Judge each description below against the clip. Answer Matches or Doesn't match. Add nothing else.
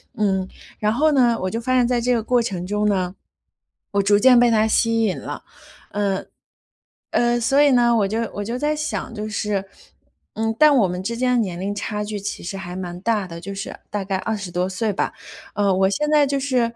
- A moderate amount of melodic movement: Matches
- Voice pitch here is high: Matches